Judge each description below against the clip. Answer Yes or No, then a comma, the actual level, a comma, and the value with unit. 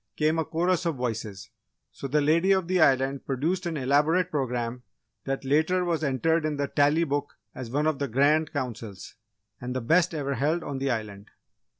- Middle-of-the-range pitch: Yes, medium, 145 Hz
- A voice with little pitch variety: No, average, 3.7 semitones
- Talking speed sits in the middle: Yes, average, 190 wpm